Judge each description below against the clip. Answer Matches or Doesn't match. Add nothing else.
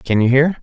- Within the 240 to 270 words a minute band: Doesn't match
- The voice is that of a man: Matches